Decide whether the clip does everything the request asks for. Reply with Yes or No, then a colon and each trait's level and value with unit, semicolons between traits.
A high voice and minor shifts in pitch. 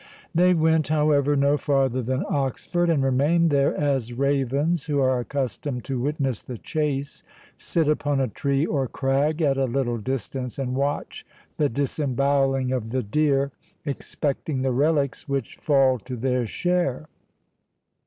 No: medium, 140 Hz; narrow, 2.2 semitones